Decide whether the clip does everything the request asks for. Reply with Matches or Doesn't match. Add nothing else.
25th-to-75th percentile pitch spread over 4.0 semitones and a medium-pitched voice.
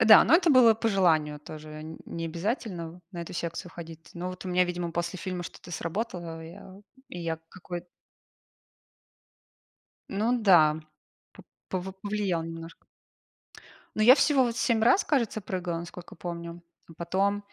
Doesn't match